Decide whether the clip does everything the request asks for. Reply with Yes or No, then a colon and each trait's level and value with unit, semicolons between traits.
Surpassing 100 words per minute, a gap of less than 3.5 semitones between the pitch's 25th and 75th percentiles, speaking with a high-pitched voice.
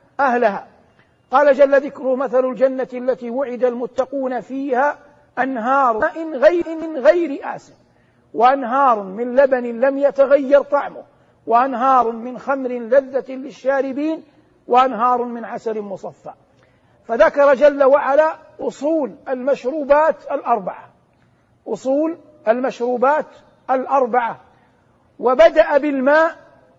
No: average, 95 wpm; narrow, 2.5 semitones; very high, 270 Hz